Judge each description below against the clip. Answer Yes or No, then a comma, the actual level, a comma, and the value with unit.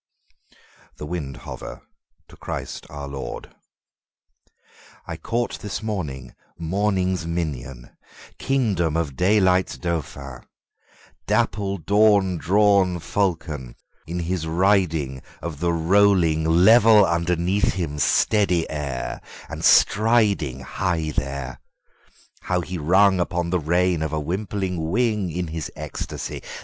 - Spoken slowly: Yes, slow, 100 wpm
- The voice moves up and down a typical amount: Yes, average, 4.2 semitones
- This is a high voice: No, very low, 85 Hz